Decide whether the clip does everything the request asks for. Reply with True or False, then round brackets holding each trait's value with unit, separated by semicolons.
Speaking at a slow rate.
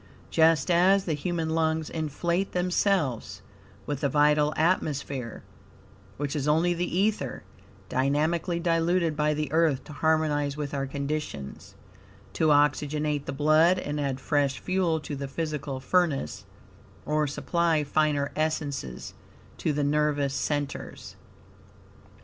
True (125 wpm)